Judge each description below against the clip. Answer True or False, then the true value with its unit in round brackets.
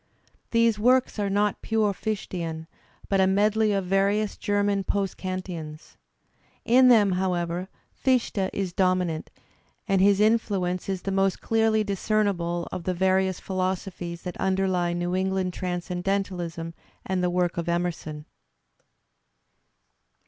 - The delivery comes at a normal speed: False (125 wpm)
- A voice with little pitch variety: True (2.3 semitones)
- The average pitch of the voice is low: False (190 Hz)